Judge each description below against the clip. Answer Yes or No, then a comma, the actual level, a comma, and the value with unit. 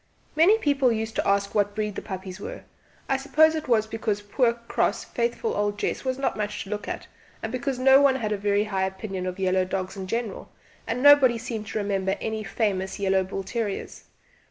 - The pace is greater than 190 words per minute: Yes, fast, 205 wpm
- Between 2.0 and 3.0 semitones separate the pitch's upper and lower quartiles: No, average, 4.3 semitones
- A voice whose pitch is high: Yes, high, 215 Hz